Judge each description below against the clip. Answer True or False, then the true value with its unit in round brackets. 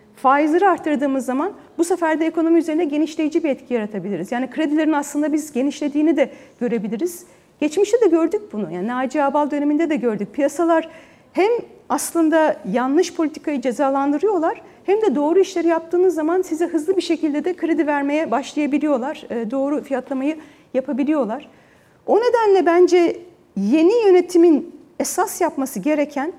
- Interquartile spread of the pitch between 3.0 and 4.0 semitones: True (3.7 semitones)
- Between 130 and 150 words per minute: True (135 wpm)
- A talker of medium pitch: False (310 Hz)